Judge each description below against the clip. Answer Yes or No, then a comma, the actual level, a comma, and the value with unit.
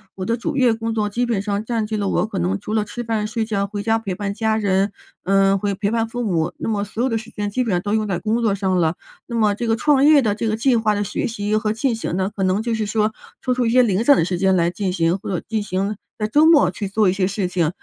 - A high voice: Yes, high, 210 Hz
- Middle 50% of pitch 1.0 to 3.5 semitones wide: Yes, narrow, 2.6 semitones